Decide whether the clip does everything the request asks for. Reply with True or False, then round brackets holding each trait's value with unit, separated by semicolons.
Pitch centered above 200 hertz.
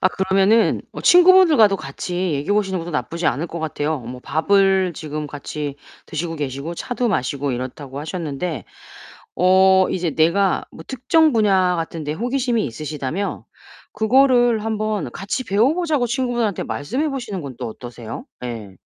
False (185 Hz)